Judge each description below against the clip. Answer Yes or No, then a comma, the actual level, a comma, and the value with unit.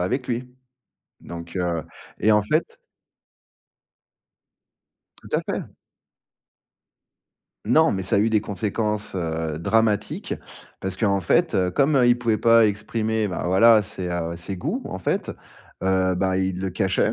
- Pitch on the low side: Yes, low, 100 Hz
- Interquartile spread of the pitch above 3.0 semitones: Yes, average, 3.5 semitones